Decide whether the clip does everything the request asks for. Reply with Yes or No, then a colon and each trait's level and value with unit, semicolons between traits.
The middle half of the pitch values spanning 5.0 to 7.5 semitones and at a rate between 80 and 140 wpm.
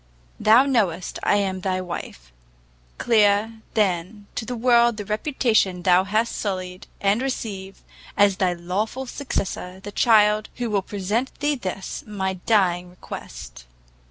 No: average, 3.3 semitones; slow, 135 wpm